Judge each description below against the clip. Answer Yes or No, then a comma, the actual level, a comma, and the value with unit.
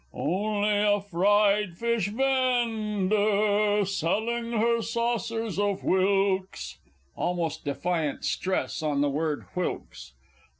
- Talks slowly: Yes, slow, 100 wpm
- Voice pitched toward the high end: Yes, high, 205 Hz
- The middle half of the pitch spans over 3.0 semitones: Yes, average, 3.5 semitones